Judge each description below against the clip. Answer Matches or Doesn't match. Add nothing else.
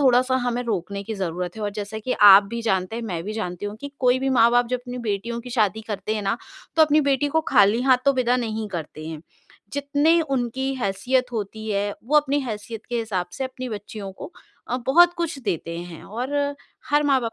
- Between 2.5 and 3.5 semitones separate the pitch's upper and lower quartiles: Doesn't match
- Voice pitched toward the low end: Doesn't match